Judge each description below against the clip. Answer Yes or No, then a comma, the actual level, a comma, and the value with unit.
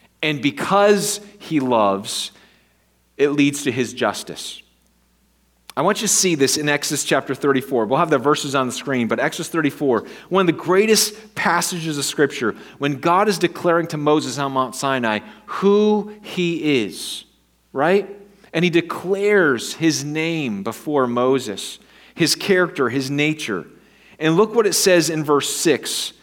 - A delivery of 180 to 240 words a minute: No, average, 155 wpm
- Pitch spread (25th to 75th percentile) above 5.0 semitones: Yes, wide, 5.4 semitones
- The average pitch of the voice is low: No, medium, 150 Hz